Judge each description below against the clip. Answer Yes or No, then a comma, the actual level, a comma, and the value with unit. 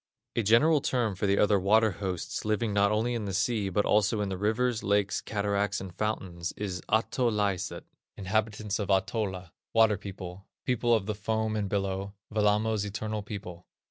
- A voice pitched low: Yes, low, 105 Hz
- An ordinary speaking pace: Yes, average, 170 wpm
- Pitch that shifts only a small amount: Yes, narrow, 2.0 semitones